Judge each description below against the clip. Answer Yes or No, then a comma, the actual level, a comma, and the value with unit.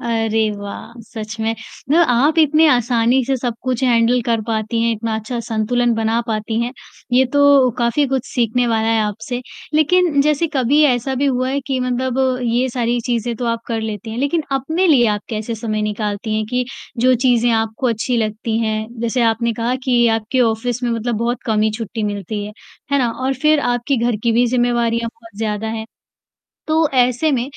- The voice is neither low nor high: No, high, 235 Hz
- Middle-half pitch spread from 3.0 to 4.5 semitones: No, narrow, 2.4 semitones